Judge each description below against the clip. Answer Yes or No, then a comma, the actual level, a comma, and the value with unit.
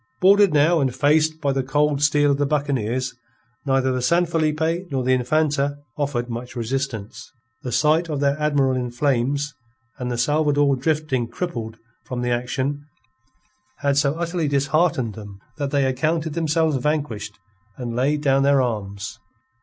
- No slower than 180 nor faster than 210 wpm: No, average, 155 wpm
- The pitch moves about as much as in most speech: Yes, average, 3.3 semitones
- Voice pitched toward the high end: No, medium, 140 Hz